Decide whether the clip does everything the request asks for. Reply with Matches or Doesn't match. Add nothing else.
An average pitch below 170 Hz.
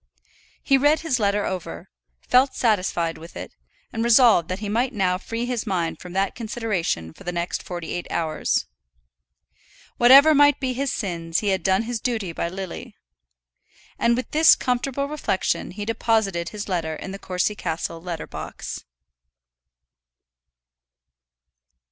Doesn't match